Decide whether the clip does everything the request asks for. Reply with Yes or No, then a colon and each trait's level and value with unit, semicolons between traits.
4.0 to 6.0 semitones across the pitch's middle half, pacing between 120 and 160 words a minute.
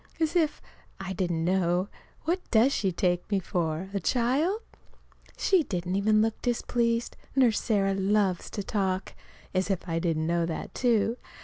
Yes: average, 4.7 semitones; average, 155 wpm